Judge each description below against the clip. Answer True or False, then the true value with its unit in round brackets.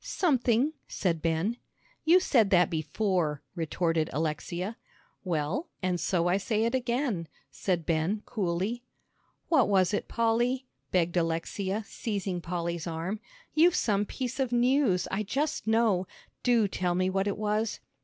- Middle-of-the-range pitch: False (195 Hz)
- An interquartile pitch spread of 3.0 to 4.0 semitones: False (5.4 semitones)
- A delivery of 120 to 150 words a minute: True (140 wpm)